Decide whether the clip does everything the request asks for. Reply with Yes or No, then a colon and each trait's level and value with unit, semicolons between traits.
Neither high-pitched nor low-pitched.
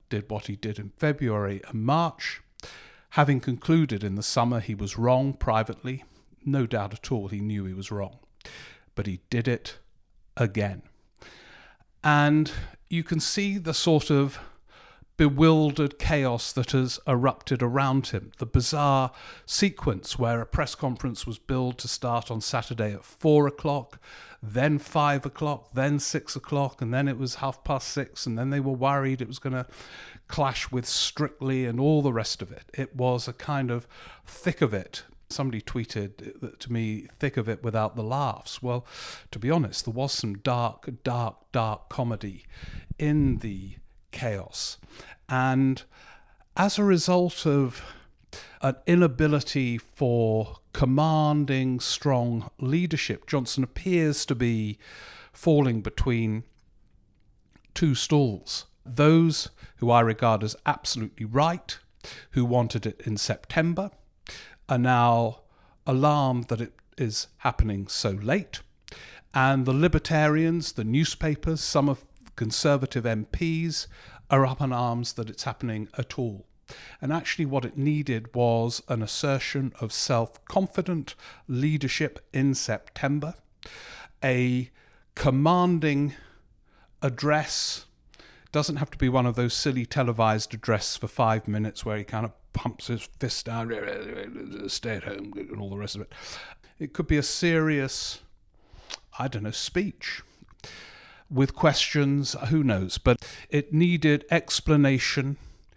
No: low, 130 Hz